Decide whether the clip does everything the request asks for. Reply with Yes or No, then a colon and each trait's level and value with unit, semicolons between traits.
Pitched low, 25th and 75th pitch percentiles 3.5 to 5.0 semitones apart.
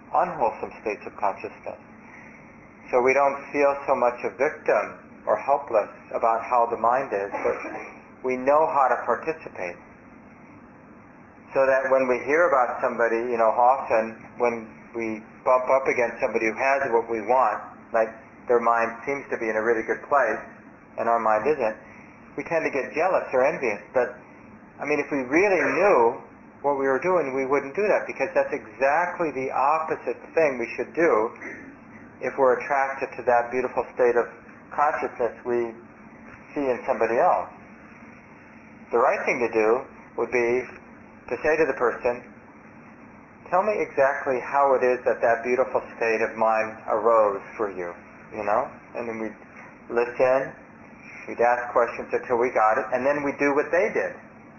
No: low, 125 Hz; average, 2.9 semitones